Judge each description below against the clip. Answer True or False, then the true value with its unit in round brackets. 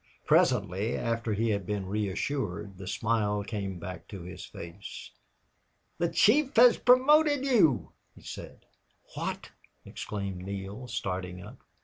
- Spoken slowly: True (125 wpm)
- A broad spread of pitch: True (5.7 semitones)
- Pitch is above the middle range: False (105 Hz)